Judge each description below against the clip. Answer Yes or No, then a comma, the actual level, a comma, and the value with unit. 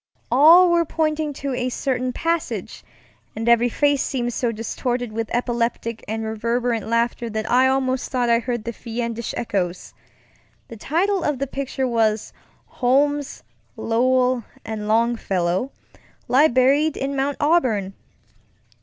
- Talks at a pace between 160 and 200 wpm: No, slow, 135 wpm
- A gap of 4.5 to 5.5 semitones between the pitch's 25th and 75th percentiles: No, average, 3.2 semitones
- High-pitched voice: Yes, high, 245 Hz